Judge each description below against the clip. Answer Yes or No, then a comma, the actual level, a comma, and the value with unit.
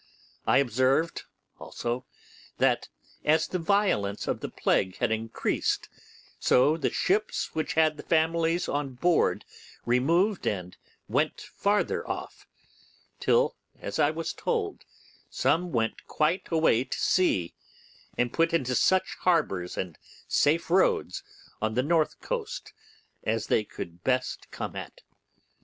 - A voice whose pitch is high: No, medium, 155 Hz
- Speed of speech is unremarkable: No, slow, 125 wpm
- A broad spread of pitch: Yes, wide, 6.6 semitones